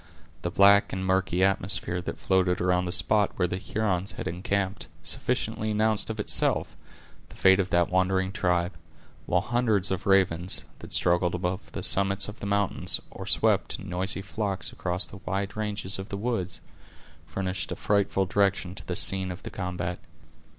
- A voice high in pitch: No, very low, 95 Hz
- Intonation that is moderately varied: No, narrow, 1.8 semitones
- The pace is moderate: Yes, average, 170 wpm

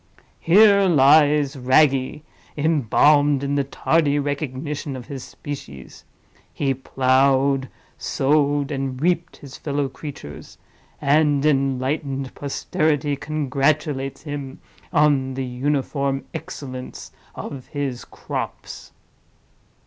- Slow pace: Yes, slow, 95 wpm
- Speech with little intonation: Yes, narrow, 1.8 semitones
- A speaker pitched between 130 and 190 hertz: Yes, medium, 140 Hz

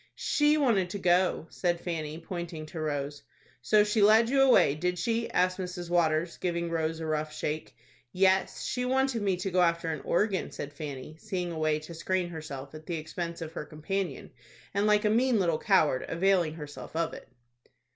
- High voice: No, medium, 175 Hz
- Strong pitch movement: No, average, 3.8 semitones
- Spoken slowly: No, average, 190 wpm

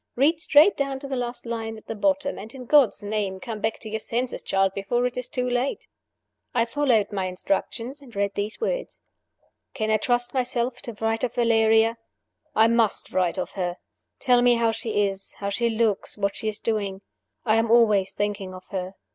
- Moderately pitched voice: No, high, 225 Hz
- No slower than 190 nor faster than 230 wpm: Yes, average, 200 wpm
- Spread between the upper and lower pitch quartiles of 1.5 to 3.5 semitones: Yes, average, 3.2 semitones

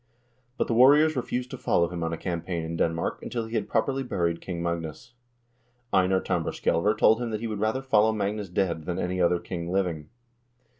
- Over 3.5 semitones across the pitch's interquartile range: Yes, average, 4.6 semitones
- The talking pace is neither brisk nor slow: Yes, average, 195 wpm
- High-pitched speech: No, very low, 95 Hz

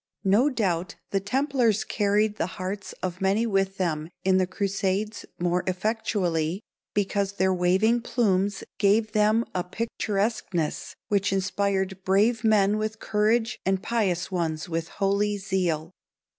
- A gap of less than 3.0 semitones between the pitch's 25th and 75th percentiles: Yes, narrow, 2.6 semitones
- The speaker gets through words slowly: Yes, slow, 130 wpm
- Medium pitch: No, high, 195 Hz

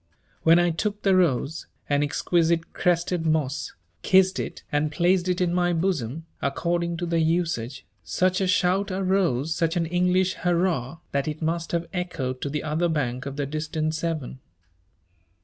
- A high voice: No, medium, 165 Hz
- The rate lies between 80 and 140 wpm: No, average, 165 wpm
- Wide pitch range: No, average, 2.9 semitones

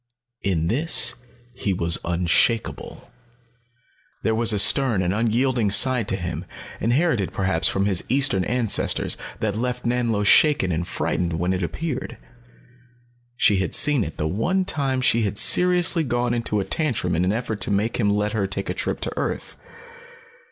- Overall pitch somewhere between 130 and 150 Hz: No, low, 110 Hz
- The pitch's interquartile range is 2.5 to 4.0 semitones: No, average, 4.7 semitones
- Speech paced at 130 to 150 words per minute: No, average, 165 wpm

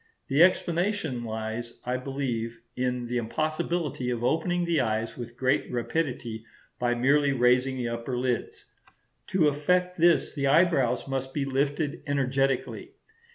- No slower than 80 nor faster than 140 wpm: Yes, slow, 135 wpm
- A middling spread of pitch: Yes, average, 4.2 semitones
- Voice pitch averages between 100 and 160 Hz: Yes, low, 135 Hz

